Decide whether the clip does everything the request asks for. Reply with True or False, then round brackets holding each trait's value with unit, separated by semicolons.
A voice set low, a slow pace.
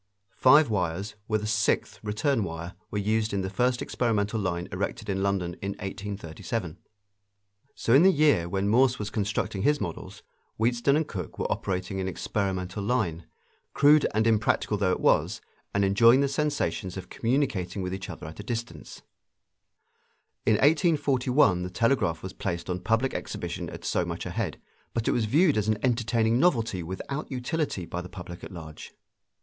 False (105 Hz; 170 wpm)